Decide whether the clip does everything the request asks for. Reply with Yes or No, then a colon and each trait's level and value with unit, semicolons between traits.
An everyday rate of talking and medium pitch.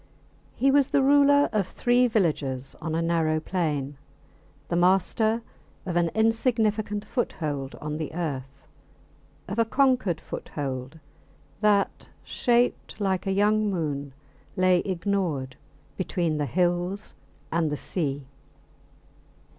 No: slow, 115 wpm; medium, 180 Hz